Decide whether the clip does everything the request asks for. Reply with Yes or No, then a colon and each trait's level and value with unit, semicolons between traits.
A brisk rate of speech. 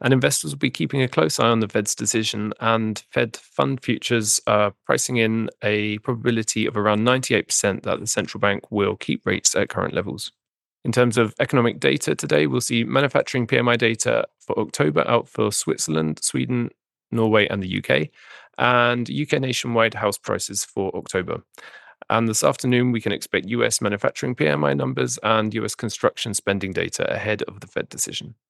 No: average, 175 wpm